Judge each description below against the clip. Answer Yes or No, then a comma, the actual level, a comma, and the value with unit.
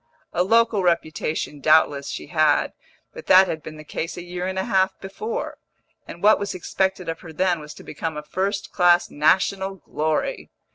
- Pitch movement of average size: Yes, average, 3.4 semitones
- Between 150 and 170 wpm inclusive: No, average, 185 wpm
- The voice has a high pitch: No, medium, 175 Hz